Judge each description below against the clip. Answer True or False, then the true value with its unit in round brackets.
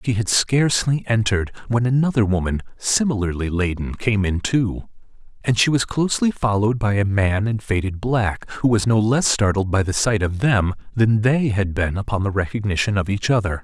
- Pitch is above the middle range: False (105 Hz)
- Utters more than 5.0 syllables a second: True (5.5 syllables/s)